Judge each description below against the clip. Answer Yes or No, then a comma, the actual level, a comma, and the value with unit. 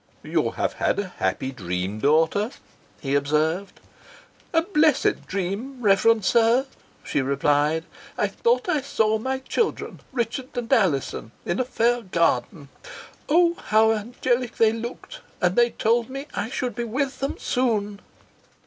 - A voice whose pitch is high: Yes, high, 225 Hz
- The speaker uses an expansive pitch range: Yes, wide, 7.3 semitones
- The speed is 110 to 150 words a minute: Yes, average, 140 wpm